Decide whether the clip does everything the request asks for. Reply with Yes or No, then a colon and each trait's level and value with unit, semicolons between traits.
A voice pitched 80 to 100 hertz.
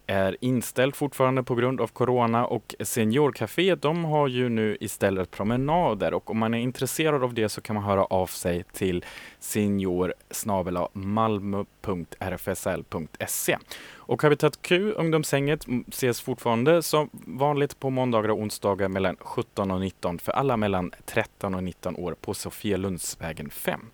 No: low, 115 Hz